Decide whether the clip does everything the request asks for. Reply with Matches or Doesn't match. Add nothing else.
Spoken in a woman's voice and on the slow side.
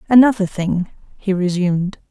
Matches